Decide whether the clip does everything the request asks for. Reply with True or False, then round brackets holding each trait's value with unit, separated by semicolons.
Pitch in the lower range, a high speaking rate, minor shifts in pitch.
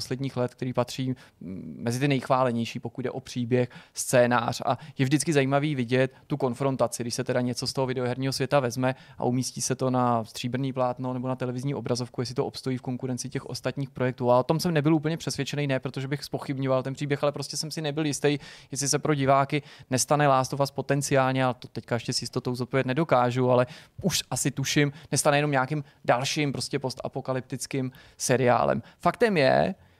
True (130 Hz; 190 wpm; 2.2 semitones)